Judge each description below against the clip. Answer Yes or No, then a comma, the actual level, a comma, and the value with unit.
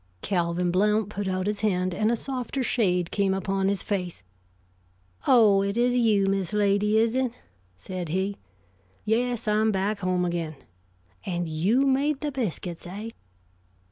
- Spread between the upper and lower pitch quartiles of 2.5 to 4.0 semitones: Yes, average, 3.5 semitones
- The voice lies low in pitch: No, high, 200 Hz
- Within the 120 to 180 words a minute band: Yes, average, 150 wpm